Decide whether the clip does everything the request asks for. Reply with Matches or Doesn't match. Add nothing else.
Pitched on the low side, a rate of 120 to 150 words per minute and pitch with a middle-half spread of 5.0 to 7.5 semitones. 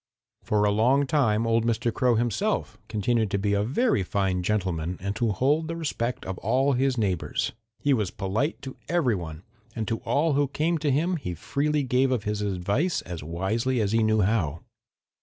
Doesn't match